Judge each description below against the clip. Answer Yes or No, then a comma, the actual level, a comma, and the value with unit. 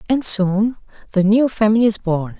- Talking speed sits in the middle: Yes, average, 175 wpm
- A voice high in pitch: Yes, high, 210 Hz